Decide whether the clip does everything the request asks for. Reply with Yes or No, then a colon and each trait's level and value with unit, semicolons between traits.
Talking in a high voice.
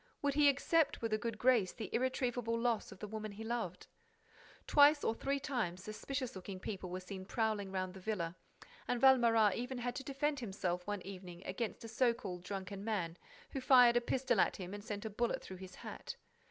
Yes: high, 220 Hz